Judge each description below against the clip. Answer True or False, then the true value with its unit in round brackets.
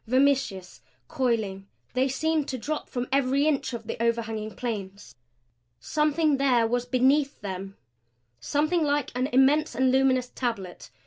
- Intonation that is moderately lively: True (3.8 semitones)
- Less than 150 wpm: True (135 wpm)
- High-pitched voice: True (255 Hz)